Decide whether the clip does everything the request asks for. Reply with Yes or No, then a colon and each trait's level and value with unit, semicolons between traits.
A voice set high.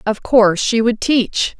Yes: high, 225 Hz